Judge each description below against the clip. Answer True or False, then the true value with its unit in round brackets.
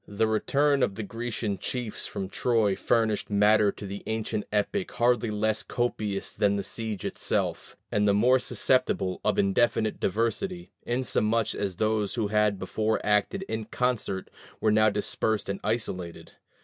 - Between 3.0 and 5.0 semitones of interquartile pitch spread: False (2.4 semitones)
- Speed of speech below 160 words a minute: True (150 wpm)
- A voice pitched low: True (110 Hz)